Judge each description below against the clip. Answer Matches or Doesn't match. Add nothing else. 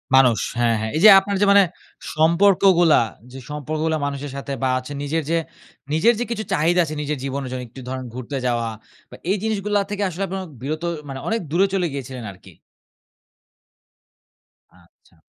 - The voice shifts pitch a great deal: Matches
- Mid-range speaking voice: Matches